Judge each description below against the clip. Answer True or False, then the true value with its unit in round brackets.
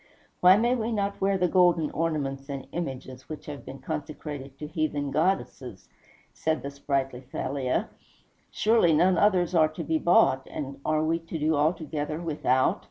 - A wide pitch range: False (3.9 semitones)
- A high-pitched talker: False (155 Hz)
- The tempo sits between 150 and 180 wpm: True (165 wpm)